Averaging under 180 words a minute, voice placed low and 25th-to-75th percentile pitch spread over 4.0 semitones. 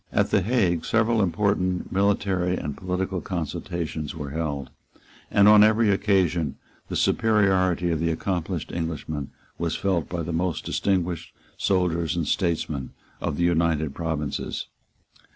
No: slow, 135 wpm; very low, 85 Hz; average, 3.0 semitones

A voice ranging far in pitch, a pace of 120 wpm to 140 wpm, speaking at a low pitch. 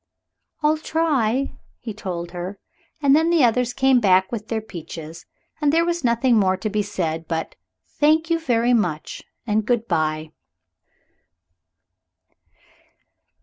No: wide, 6.9 semitones; slow, 135 wpm; high, 225 Hz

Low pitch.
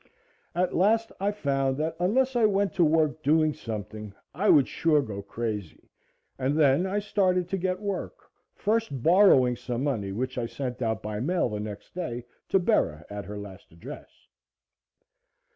No: medium, 145 Hz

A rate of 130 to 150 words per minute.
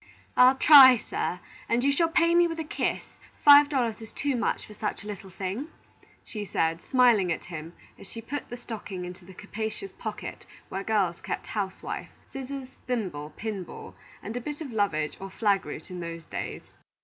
No: average, 190 wpm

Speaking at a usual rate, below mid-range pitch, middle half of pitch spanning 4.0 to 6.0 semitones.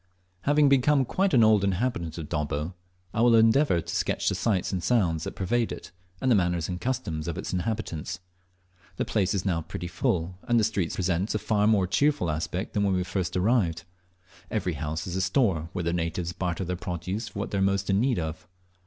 No: fast, 215 wpm; very low, 95 Hz; average, 4.6 semitones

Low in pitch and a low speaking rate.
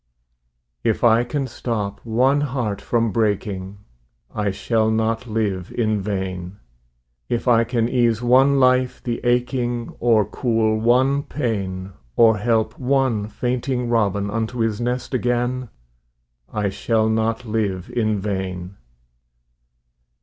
Yes: low, 115 Hz; slow, 120 wpm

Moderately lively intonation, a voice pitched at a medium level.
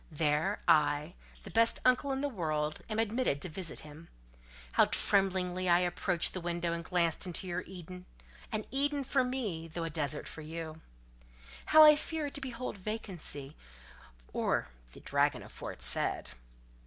No: wide, 6.2 semitones; medium, 175 Hz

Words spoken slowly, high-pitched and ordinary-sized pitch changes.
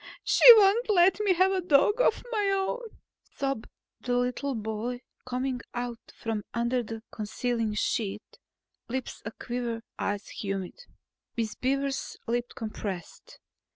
No: slow, 125 wpm; high, 245 Hz; wide, 7.8 semitones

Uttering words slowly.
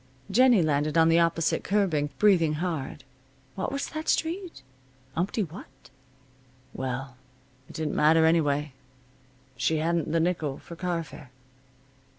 Yes: slow, 130 wpm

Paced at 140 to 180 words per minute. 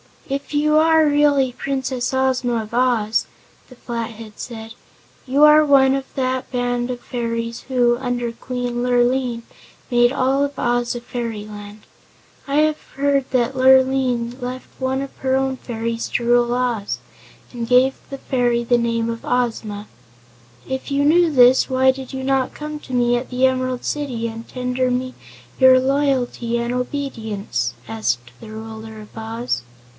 Yes: average, 155 wpm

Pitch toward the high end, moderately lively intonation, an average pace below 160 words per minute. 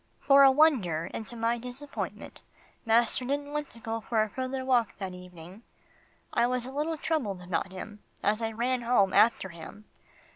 No: high, 235 Hz; average, 4.5 semitones; average, 180 wpm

